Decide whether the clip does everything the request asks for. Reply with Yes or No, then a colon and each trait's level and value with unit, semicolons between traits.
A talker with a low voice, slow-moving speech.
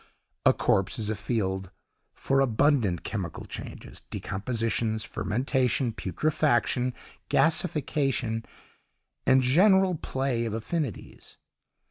Yes: low, 125 Hz; slow, 90 wpm